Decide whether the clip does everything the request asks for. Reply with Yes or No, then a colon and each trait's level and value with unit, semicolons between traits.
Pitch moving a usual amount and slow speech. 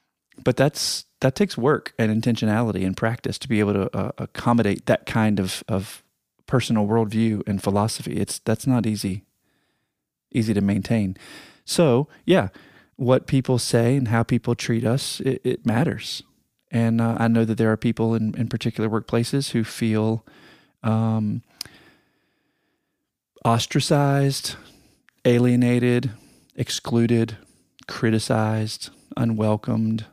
No: narrow, 2.1 semitones; slow, 125 wpm